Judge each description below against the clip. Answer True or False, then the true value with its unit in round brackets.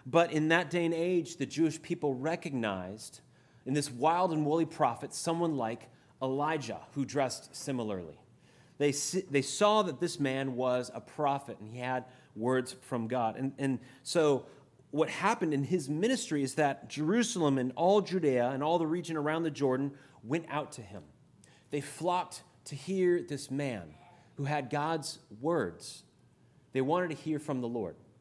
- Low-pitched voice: False (145 Hz)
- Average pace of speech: True (170 wpm)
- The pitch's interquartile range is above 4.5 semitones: False (4.1 semitones)